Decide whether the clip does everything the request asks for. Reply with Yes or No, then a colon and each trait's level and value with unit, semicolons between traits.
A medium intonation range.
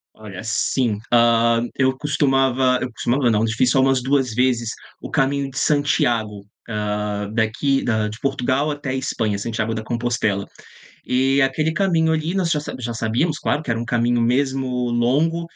Yes: average, 3.6 semitones